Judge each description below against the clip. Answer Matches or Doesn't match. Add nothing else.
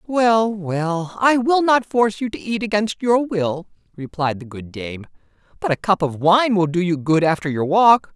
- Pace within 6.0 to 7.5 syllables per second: Doesn't match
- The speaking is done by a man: Matches